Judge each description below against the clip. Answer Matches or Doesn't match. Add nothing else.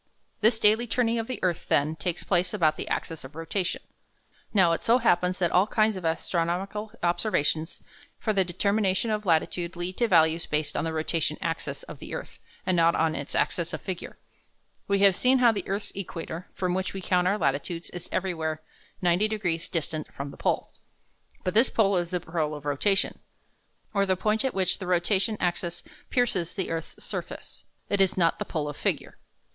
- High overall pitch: Doesn't match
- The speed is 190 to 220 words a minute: Matches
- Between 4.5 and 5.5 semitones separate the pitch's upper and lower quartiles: Doesn't match